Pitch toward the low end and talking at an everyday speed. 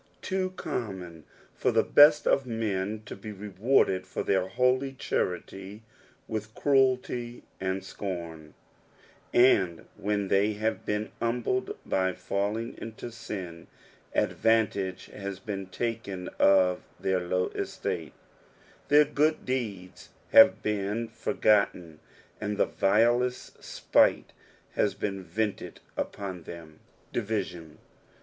No: low, 105 Hz; slow, 115 wpm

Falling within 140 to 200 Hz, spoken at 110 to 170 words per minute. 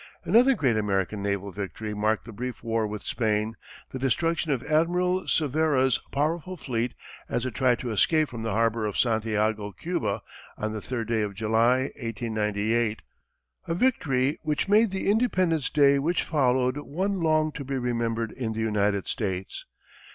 No: low, 120 Hz; average, 160 wpm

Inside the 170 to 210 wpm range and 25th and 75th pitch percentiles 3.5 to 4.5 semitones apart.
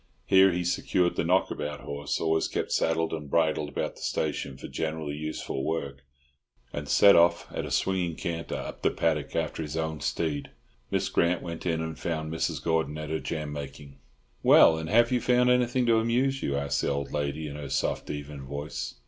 No: average, 195 wpm; average, 3.1 semitones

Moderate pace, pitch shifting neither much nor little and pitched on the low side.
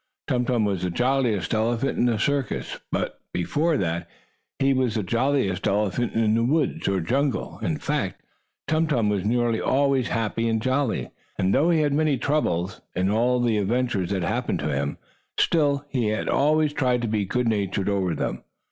Yes: average, 180 wpm; average, 5.0 semitones; low, 120 Hz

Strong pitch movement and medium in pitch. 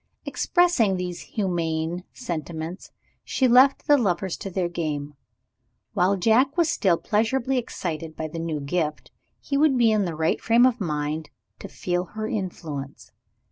Yes: wide, 6.4 semitones; medium, 180 Hz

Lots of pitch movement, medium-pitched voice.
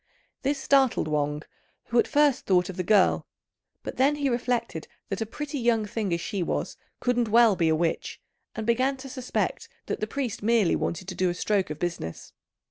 No: wide, 6.0 semitones; high, 220 Hz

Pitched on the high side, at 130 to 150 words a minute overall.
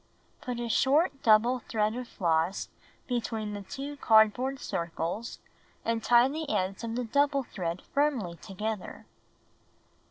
Yes: high, 230 Hz; slow, 135 wpm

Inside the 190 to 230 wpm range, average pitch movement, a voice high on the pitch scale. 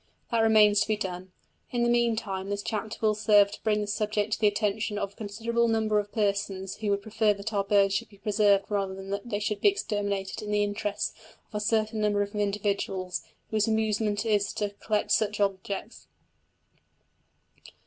No: average, 195 wpm; narrow, 1.3 semitones; high, 210 Hz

